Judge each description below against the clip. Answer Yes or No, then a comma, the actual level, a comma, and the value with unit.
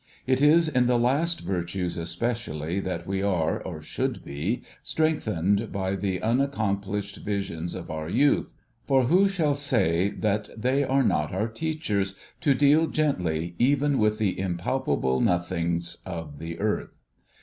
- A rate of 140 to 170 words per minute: Yes, average, 145 wpm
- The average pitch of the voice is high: No, low, 100 Hz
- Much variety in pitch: Yes, wide, 7.4 semitones